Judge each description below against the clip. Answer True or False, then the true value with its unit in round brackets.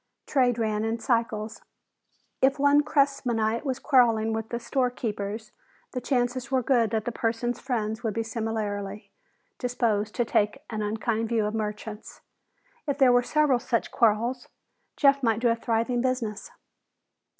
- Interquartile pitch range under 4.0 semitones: True (2.4 semitones)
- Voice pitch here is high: True (230 Hz)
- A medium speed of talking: True (150 wpm)